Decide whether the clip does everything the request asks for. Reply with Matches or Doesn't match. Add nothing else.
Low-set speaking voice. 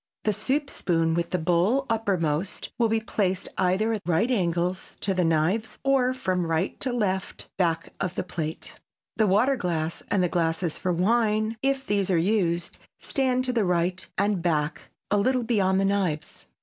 Doesn't match